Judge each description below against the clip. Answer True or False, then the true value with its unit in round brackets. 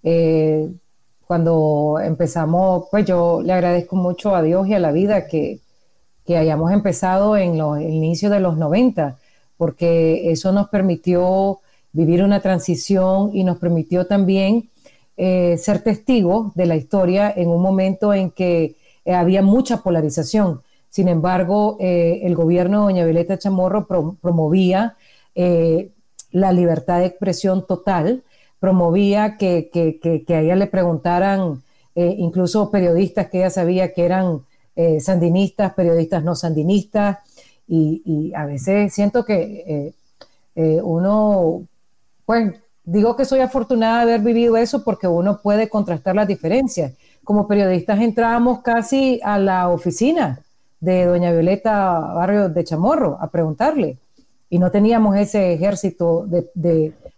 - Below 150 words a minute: True (140 wpm)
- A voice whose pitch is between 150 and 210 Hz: True (185 Hz)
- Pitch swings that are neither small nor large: True (3.3 semitones)